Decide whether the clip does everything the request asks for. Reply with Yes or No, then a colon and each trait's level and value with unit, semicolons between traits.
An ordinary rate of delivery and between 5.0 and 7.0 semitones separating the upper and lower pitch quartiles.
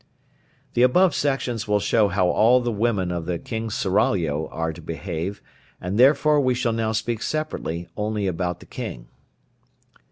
Yes: average, 160 wpm; wide, 5.4 semitones